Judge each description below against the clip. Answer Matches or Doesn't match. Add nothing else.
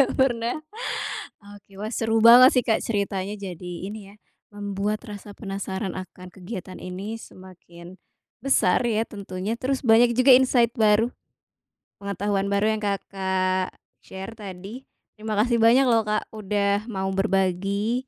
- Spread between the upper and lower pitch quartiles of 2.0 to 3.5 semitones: Matches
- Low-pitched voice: Doesn't match